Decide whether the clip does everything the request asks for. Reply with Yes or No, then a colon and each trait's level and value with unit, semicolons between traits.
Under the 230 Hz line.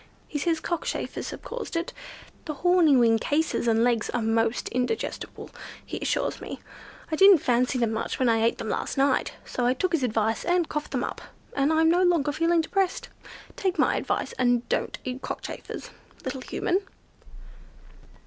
No: very high, 280 Hz